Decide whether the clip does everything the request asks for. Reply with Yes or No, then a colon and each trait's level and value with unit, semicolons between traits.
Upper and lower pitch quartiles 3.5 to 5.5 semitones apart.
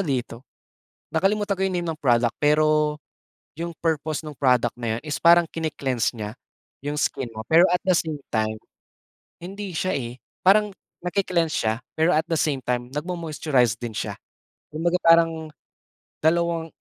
Yes: average, 5.0 semitones